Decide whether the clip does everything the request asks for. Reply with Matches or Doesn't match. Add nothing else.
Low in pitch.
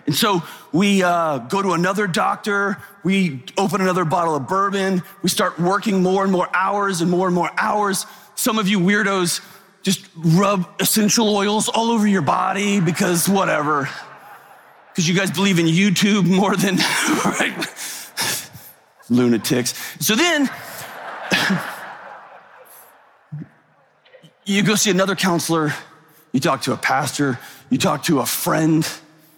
Doesn't match